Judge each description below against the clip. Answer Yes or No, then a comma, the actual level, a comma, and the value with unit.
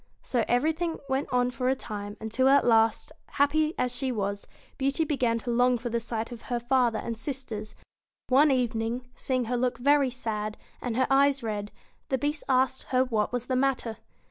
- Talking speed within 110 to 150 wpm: No, average, 200 wpm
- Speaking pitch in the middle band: No, very high, 250 Hz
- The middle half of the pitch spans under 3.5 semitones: Yes, average, 2.8 semitones